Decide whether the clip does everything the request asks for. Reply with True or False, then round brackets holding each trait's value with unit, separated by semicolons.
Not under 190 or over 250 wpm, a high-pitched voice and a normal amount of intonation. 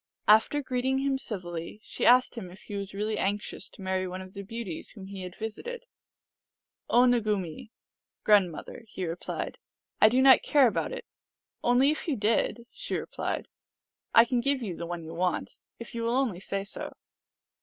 True (195 wpm; 215 Hz; 4.9 semitones)